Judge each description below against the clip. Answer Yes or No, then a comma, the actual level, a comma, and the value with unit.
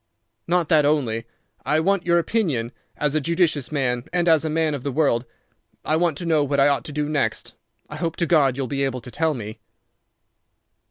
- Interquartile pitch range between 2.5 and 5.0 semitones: Yes, average, 3.4 semitones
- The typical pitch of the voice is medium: Yes, medium, 150 Hz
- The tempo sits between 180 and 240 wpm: Yes, average, 200 wpm